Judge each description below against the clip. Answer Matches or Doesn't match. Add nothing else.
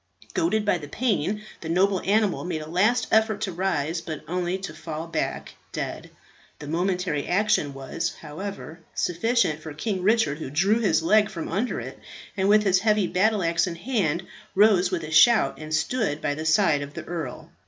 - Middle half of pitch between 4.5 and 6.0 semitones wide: Matches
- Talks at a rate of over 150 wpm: Matches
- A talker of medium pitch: Matches